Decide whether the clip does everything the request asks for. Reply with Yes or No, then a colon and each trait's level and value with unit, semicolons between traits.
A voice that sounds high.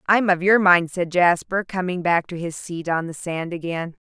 No: medium, 175 Hz